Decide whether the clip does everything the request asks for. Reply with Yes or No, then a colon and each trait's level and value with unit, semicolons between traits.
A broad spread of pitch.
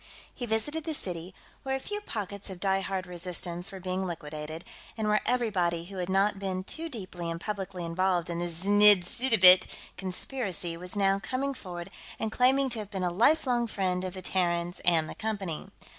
No: average, 3.7 semitones